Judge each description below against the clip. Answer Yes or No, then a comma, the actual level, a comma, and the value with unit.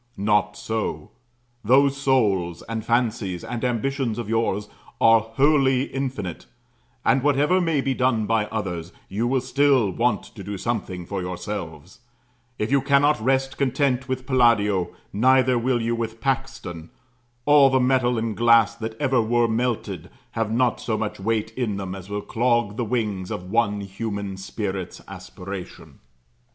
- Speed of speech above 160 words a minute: No, average, 150 wpm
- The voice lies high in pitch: No, low, 115 Hz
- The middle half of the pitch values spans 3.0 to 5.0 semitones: Yes, average, 4.1 semitones